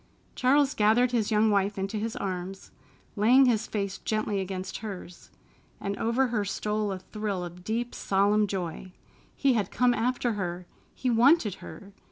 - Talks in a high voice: Yes, high, 210 Hz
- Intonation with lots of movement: No, average, 3.3 semitones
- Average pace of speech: Yes, average, 160 wpm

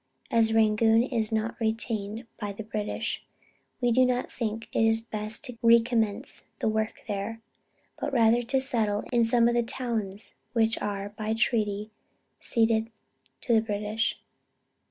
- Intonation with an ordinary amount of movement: No, narrow, 1.6 semitones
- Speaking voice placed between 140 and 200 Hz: No, high, 225 Hz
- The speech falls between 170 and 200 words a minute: No, average, 145 wpm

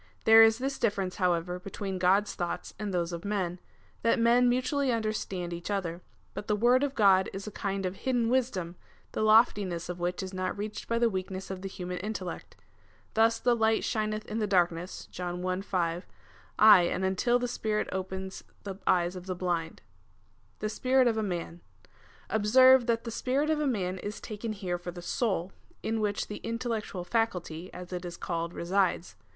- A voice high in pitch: Yes, high, 195 Hz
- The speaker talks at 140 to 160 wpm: No, average, 185 wpm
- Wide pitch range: No, average, 3.9 semitones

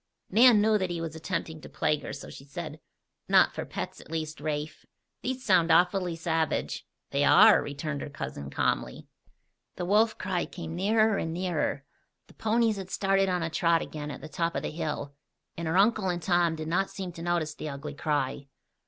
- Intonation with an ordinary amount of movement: Yes, average, 3.7 semitones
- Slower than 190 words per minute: No, average, 195 wpm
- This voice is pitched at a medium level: Yes, medium, 170 Hz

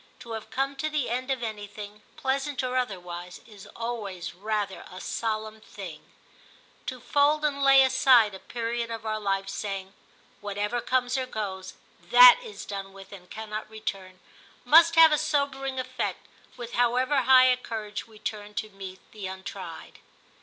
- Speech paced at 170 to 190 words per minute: Yes, average, 175 wpm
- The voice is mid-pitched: No, high, 225 Hz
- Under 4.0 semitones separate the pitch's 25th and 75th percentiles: No, average, 4.3 semitones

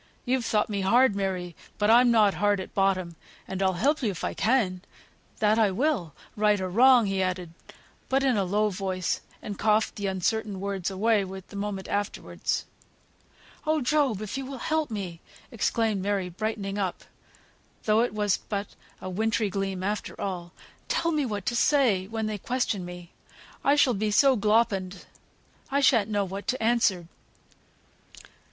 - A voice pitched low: No, high, 205 Hz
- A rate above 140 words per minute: Yes, average, 170 wpm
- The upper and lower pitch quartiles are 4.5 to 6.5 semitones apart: No, average, 3.3 semitones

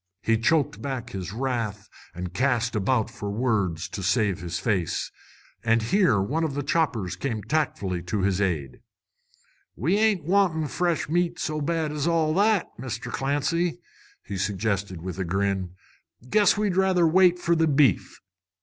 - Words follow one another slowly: No, average, 160 wpm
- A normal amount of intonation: No, wide, 8.5 semitones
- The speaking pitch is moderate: No, low, 125 Hz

